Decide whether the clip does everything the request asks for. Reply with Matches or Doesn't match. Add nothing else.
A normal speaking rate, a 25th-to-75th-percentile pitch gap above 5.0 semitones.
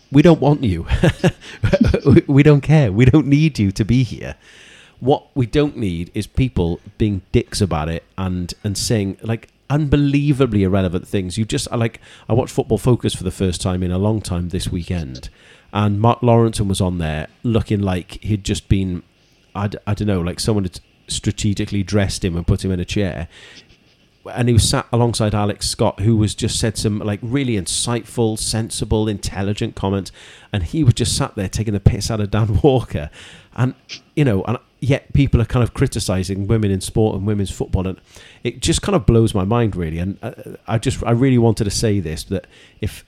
Doesn't match